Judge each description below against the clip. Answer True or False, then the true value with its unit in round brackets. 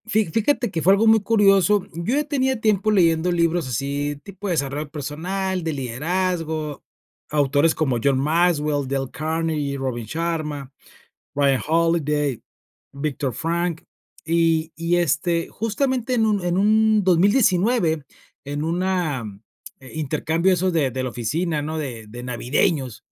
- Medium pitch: True (165 Hz)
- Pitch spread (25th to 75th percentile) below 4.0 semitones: False (4.6 semitones)